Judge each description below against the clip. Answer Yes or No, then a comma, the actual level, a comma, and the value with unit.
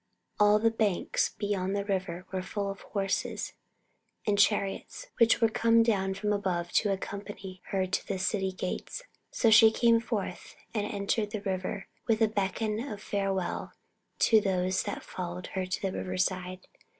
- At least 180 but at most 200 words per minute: No, average, 165 wpm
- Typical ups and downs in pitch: No, narrow, 2.3 semitones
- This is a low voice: No, high, 200 Hz